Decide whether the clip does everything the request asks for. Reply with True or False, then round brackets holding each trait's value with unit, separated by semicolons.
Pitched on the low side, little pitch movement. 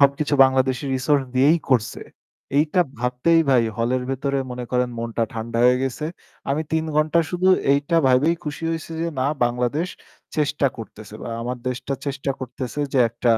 False (130 Hz; 3.2 semitones)